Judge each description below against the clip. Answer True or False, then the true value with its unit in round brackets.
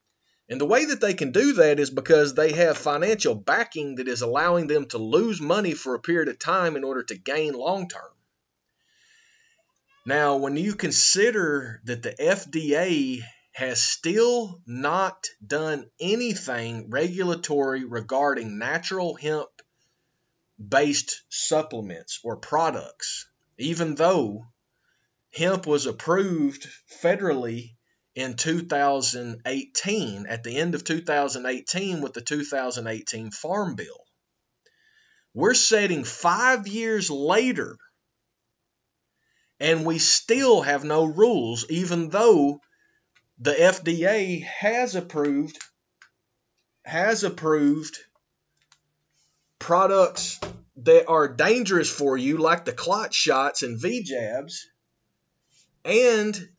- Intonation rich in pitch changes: True (5.9 semitones)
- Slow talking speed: True (110 wpm)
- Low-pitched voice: False (155 Hz)